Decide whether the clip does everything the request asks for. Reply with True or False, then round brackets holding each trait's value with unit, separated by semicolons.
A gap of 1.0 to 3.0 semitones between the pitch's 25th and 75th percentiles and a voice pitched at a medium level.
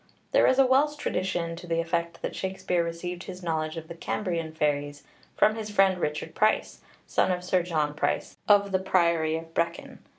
True (2.5 semitones; 170 Hz)